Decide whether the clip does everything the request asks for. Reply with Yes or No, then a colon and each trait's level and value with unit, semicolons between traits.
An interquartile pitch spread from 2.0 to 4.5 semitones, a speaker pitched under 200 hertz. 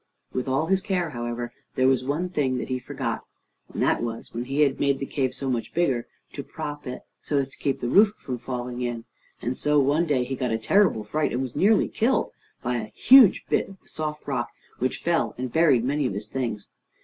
Yes: average, 3.8 semitones; low, 135 Hz